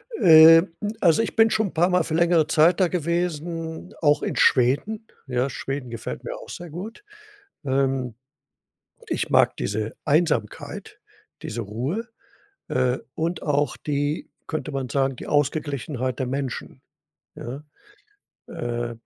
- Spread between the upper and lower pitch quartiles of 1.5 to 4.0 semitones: No, average, 4.5 semitones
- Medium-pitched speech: Yes, medium, 150 Hz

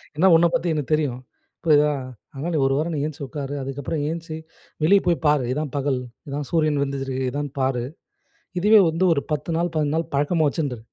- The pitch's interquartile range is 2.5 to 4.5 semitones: Yes, average, 2.8 semitones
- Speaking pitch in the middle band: Yes, medium, 150 Hz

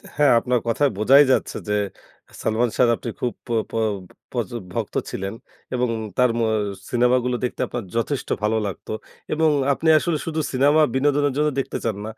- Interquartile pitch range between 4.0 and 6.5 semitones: No, average, 3.6 semitones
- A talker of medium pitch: No, low, 125 Hz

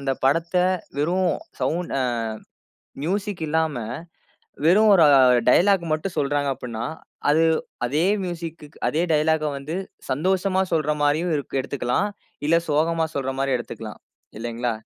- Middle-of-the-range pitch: Yes, medium, 155 Hz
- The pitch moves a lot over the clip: No, average, 3.8 semitones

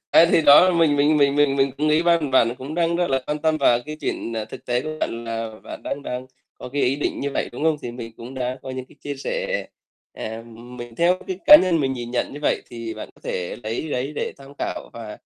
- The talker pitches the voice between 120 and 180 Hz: Yes, medium, 140 Hz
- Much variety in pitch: No, average, 4.4 semitones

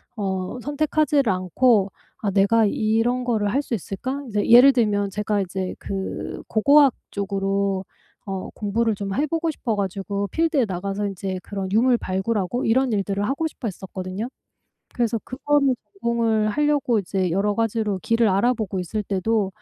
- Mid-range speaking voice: No, high, 210 Hz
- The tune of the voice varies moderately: Yes, average, 3.8 semitones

